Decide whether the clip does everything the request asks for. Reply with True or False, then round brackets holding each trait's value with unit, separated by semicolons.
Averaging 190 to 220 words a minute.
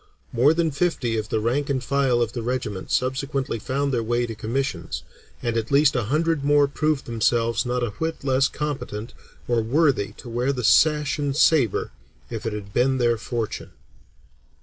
False (175 wpm)